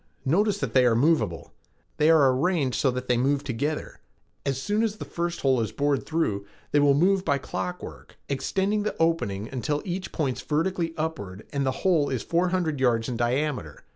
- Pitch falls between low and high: Yes, medium, 145 Hz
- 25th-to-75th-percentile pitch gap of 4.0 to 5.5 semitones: Yes, average, 5.0 semitones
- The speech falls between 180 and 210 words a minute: Yes, average, 190 wpm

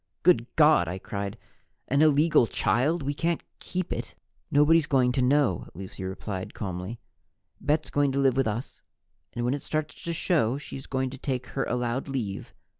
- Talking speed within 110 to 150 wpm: No, average, 175 wpm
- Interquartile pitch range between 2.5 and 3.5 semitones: No, average, 4.6 semitones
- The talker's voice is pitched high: No, low, 135 Hz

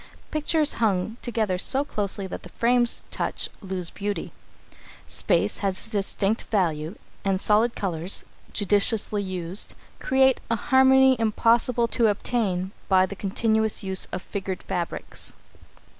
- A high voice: Yes, high, 205 Hz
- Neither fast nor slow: No, slow, 125 wpm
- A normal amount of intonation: Yes, average, 3.7 semitones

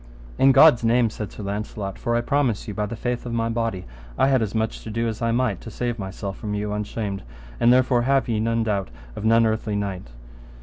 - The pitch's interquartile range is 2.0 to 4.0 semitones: Yes, narrow, 2.4 semitones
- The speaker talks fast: Yes, fast, 230 wpm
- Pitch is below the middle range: Yes, low, 115 Hz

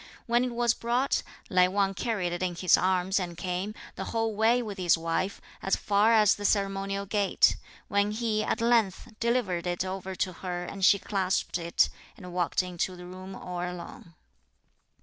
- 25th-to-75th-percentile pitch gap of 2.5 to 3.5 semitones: Yes, average, 3.0 semitones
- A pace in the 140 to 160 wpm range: No, average, 180 wpm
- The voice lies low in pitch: No, high, 195 Hz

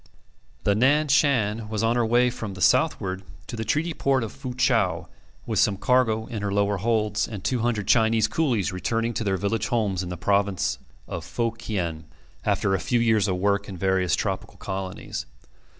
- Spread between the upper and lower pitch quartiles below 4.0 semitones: Yes, average, 3.3 semitones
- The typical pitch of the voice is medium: No, low, 110 Hz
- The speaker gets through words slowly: No, average, 190 wpm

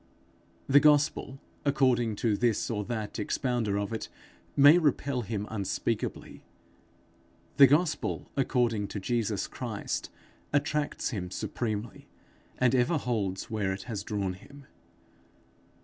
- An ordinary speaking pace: No, slow, 115 wpm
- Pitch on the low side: Yes, low, 120 Hz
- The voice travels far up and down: No, average, 5.0 semitones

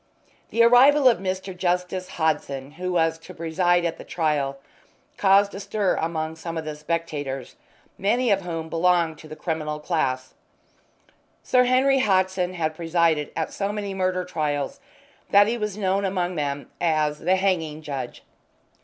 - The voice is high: No, medium, 175 Hz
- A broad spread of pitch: No, average, 3.7 semitones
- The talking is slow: No, average, 155 wpm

